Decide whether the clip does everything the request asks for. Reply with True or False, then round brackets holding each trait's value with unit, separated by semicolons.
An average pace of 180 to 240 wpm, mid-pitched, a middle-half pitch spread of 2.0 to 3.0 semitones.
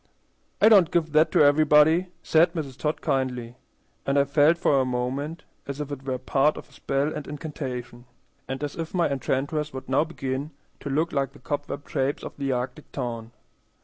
True (190 wpm; 145 Hz; 2.6 semitones)